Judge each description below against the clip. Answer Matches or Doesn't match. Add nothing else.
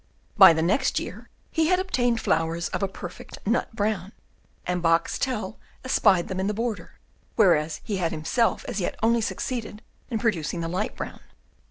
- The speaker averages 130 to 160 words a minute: Doesn't match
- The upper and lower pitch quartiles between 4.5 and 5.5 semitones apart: Matches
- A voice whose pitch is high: Matches